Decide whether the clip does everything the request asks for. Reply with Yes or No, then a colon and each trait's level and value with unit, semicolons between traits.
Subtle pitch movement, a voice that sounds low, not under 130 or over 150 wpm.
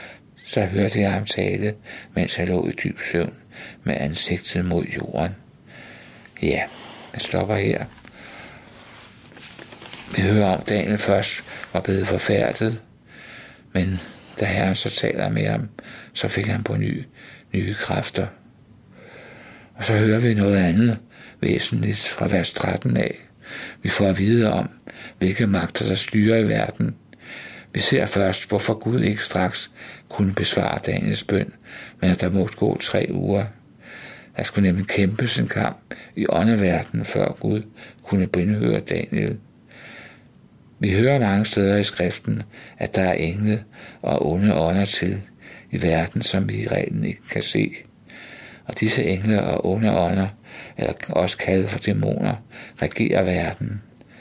Yes: narrow, 2.3 semitones; low, 100 Hz; slow, 145 wpm